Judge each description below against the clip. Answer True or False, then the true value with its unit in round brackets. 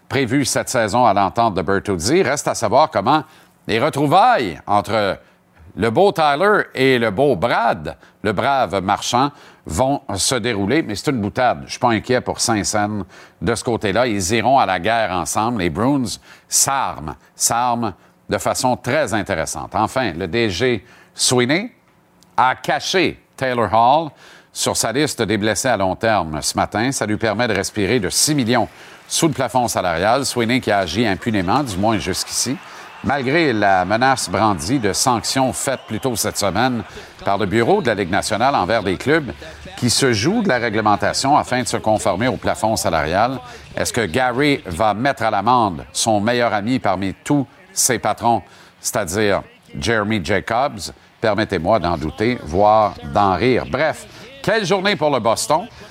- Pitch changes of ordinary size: True (3.9 semitones)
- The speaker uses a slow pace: False (165 wpm)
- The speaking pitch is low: True (115 Hz)